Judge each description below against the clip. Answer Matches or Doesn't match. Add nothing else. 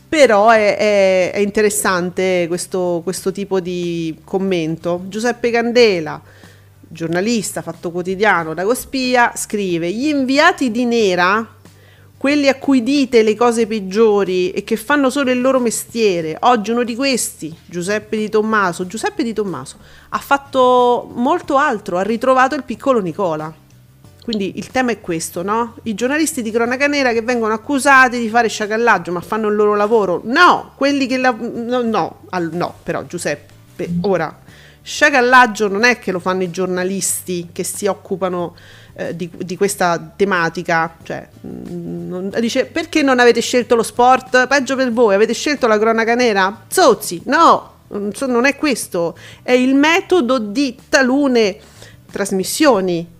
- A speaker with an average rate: Matches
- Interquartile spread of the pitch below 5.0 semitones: Doesn't match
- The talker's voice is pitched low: Doesn't match